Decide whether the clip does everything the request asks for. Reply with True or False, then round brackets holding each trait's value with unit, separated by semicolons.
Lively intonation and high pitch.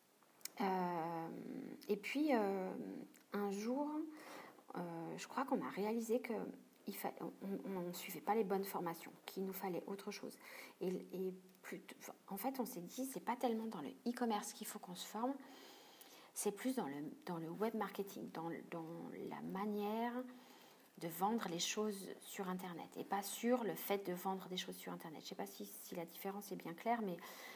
False (4.2 semitones; 200 Hz)